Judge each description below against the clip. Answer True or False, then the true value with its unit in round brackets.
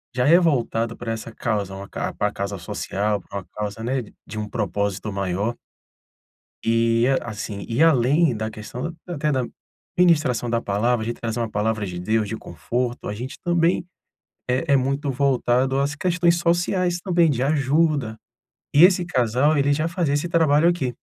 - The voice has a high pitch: False (125 Hz)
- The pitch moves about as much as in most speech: False (5.8 semitones)